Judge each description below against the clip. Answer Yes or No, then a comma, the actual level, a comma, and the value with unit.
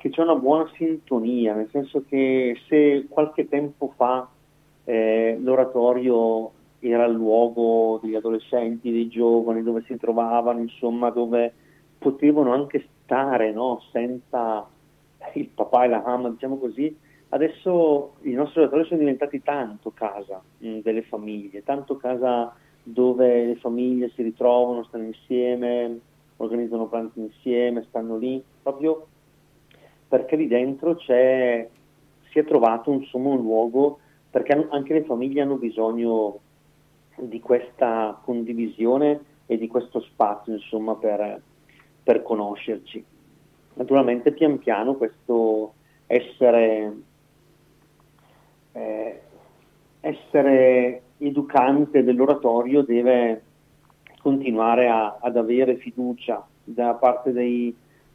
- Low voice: Yes, low, 125 Hz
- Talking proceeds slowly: Yes, slow, 110 wpm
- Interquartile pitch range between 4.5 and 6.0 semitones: No, average, 3.3 semitones